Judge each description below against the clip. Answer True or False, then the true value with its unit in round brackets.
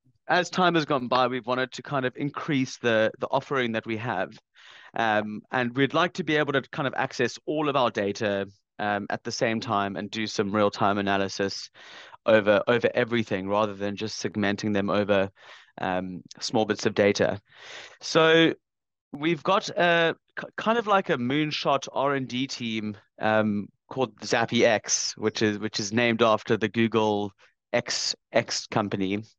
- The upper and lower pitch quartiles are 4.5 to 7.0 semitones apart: True (5.1 semitones)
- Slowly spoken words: False (175 wpm)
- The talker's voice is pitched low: True (115 Hz)